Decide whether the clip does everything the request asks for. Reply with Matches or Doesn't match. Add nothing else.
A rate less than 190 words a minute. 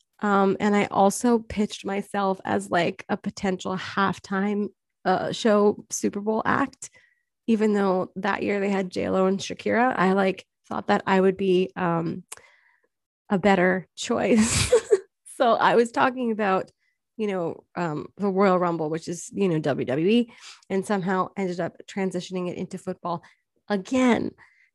Matches